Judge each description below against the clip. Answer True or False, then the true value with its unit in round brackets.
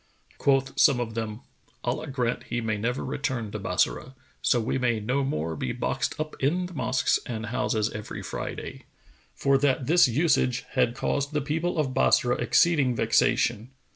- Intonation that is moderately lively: True (3.5 semitones)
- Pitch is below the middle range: True (130 Hz)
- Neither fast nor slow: True (170 wpm)